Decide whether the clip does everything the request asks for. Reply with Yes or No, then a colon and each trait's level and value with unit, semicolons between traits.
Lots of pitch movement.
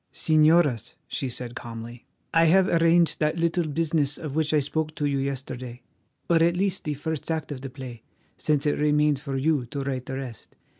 No: average, 3.3 semitones